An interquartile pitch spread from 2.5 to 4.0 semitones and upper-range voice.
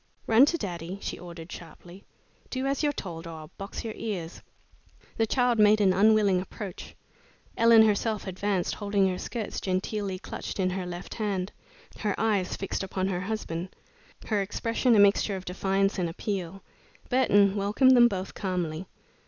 Yes: average, 2.9 semitones; high, 195 Hz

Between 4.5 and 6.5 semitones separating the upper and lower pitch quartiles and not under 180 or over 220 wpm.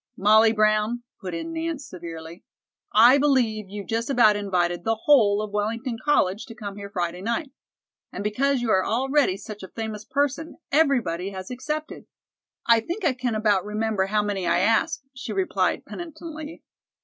No: average, 5.1 semitones; average, 165 wpm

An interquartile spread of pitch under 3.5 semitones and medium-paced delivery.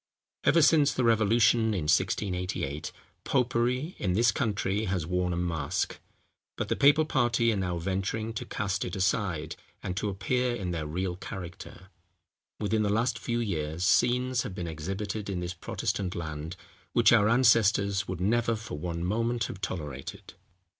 No: average, 4.7 semitones; average, 160 wpm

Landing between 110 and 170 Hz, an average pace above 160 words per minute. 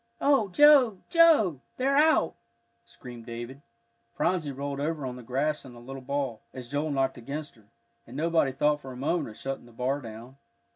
Yes: medium, 140 Hz; average, 185 wpm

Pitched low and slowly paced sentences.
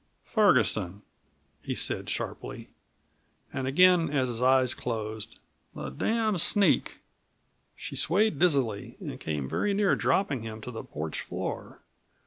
Yes: low, 130 Hz; slow, 125 wpm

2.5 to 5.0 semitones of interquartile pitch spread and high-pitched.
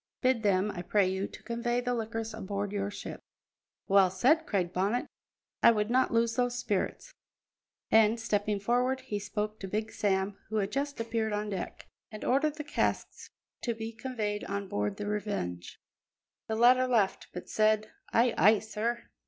Yes: average, 2.8 semitones; high, 215 Hz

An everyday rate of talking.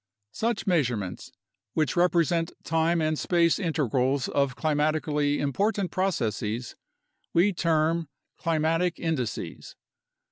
No: slow, 95 wpm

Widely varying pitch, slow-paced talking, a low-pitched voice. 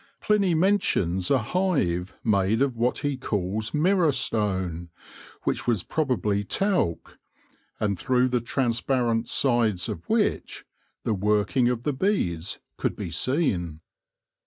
Yes: wide, 6.1 semitones; slow, 125 wpm; low, 115 Hz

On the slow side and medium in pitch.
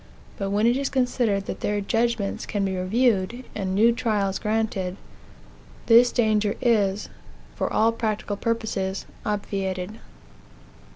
No: slow, 125 wpm; high, 210 Hz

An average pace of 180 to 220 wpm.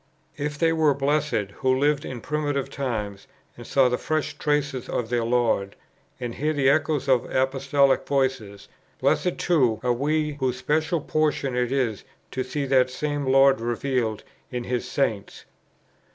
No: average, 155 wpm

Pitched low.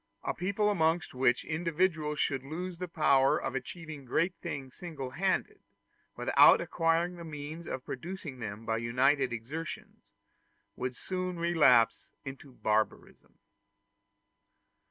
No: medium, 155 Hz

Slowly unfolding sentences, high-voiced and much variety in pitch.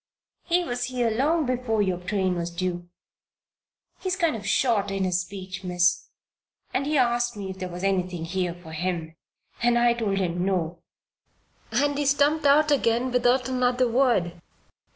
No: average, 165 wpm; high, 215 Hz; wide, 5.8 semitones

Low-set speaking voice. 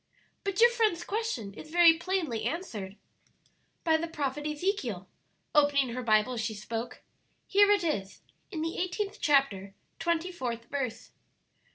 No: very high, 300 Hz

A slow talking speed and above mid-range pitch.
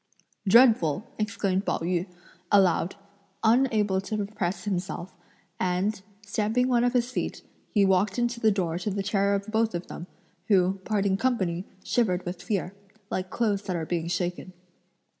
No: average, 155 wpm; high, 195 Hz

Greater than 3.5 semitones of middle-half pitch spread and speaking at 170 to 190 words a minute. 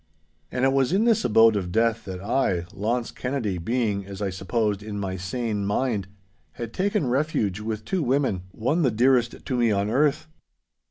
Yes: average, 4.5 semitones; average, 180 wpm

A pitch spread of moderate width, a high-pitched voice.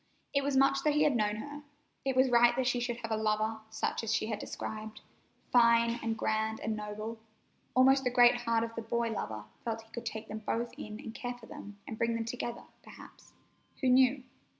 No: narrow, 2.2 semitones; high, 230 Hz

